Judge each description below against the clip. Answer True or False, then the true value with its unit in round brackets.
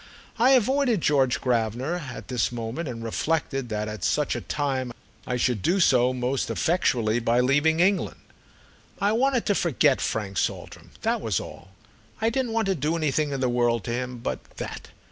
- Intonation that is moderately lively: False (6.3 semitones)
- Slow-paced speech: False (175 wpm)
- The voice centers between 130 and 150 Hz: True (135 Hz)